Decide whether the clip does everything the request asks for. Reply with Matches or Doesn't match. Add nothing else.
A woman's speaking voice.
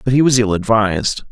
Doesn't match